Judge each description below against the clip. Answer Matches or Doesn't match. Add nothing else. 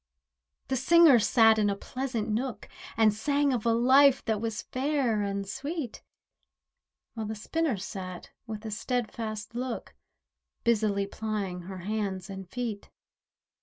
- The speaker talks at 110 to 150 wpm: Matches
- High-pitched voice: Matches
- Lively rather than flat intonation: Doesn't match